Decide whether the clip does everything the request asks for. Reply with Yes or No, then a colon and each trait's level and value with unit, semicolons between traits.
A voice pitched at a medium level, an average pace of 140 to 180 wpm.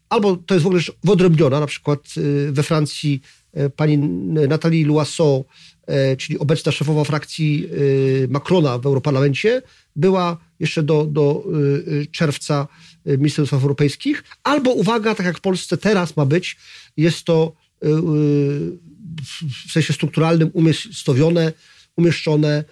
No: medium, 155 Hz; average, 115 wpm